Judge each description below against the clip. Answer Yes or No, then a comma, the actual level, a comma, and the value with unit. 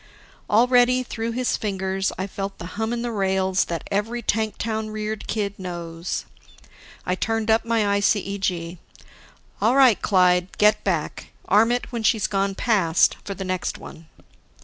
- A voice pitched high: Yes, high, 205 Hz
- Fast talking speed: No, average, 155 wpm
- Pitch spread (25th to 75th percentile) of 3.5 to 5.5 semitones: No, average, 3.0 semitones